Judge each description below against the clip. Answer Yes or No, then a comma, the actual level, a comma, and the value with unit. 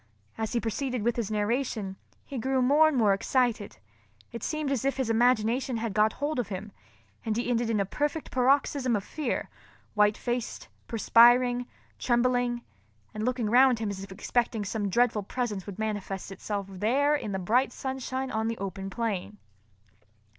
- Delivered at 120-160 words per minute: No, average, 170 wpm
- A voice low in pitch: No, high, 235 Hz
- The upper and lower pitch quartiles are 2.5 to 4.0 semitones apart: Yes, average, 3.4 semitones